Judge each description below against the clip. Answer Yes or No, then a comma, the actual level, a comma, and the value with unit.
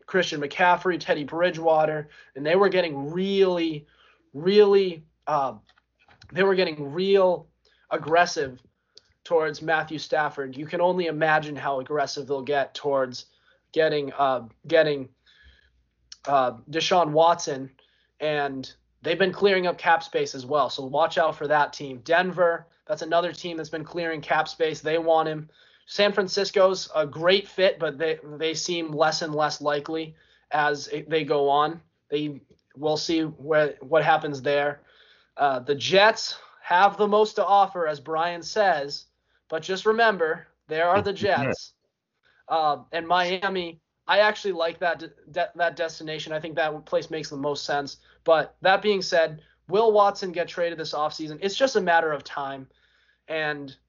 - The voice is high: No, medium, 160 Hz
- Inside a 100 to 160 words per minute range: Yes, average, 155 wpm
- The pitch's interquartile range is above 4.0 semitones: No, average, 3.2 semitones